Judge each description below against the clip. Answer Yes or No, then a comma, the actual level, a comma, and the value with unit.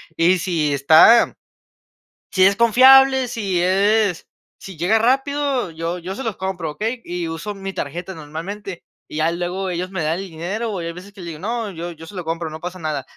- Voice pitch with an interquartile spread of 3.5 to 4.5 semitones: Yes, average, 4.1 semitones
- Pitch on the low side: No, medium, 185 Hz